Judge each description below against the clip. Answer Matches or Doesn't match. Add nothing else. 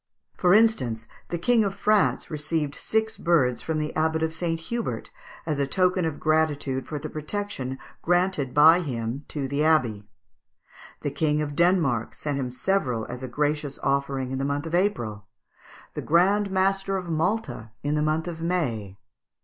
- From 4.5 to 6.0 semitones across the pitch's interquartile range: Matches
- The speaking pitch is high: Doesn't match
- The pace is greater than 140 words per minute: Matches